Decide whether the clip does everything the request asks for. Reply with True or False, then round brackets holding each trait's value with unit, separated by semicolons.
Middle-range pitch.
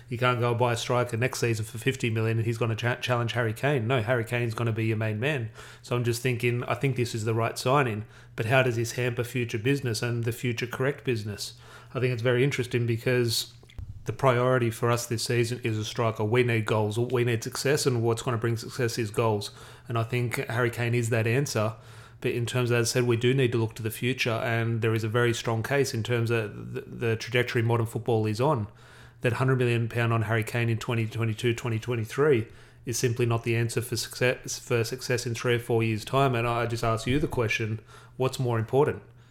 False (120 Hz)